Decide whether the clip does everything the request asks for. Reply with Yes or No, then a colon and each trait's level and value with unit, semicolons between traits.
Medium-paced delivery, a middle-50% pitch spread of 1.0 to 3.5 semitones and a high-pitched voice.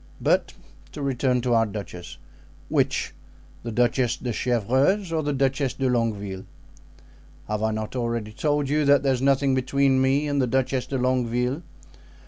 No: average, 155 wpm; average, 2.9 semitones; low, 130 Hz